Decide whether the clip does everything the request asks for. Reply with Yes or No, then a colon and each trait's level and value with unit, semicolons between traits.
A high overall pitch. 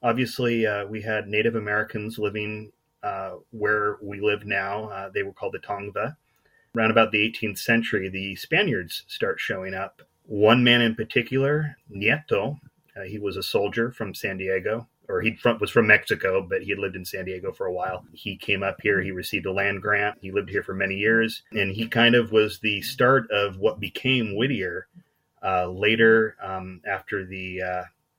No: low, 110 Hz